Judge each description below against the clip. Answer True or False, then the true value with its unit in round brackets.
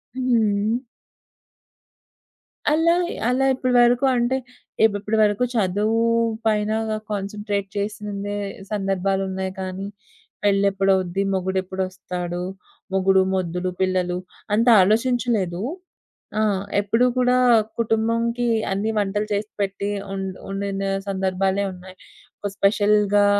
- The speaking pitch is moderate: False (200 Hz)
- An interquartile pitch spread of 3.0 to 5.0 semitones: False (2.5 semitones)